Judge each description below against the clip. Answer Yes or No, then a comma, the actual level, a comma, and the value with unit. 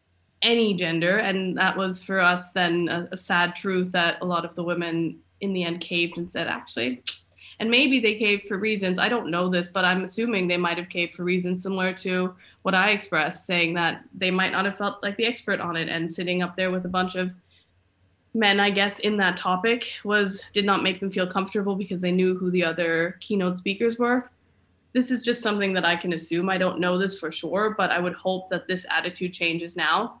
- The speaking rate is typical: No, fast, 225 wpm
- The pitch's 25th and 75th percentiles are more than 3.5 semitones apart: No, narrow, 2.4 semitones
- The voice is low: No, medium, 185 Hz